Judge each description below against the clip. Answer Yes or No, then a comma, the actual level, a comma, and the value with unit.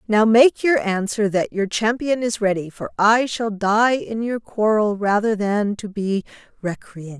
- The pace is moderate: Yes, average, 175 wpm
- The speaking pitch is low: No, high, 210 Hz